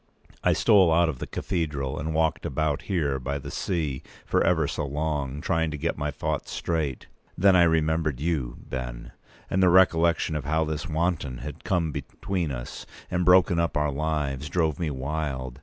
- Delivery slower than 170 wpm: No, average, 180 wpm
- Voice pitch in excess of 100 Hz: No, very low, 80 Hz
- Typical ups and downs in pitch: Yes, average, 3.0 semitones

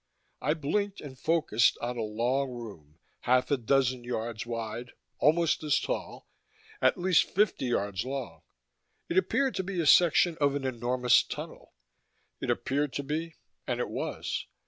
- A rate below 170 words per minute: Yes, average, 155 wpm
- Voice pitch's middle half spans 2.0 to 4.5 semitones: No, average, 5.2 semitones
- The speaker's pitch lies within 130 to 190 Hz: Yes, low, 135 Hz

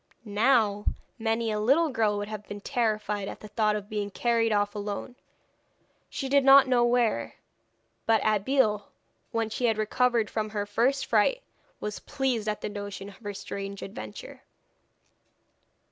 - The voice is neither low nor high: No, high, 215 Hz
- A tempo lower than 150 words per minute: No, average, 155 wpm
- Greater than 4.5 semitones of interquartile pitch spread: No, average, 2.7 semitones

